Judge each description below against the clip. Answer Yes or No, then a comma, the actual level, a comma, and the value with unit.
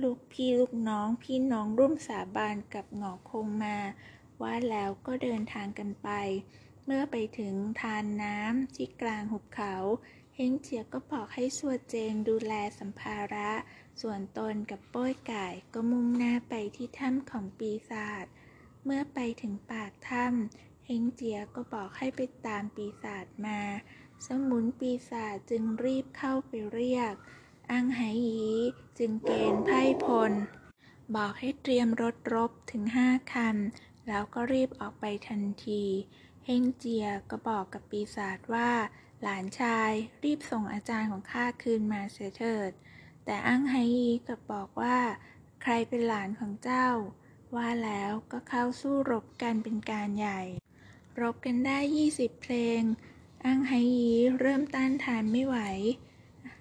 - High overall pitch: Yes, high, 230 Hz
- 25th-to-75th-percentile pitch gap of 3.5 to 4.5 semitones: No, average, 3.0 semitones